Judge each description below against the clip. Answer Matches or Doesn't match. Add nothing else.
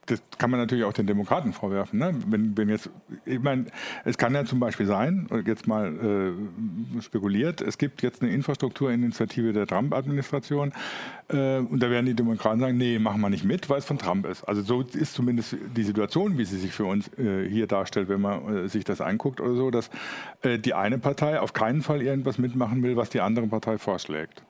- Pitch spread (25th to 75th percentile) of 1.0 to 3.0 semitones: Doesn't match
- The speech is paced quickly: Matches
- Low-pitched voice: Matches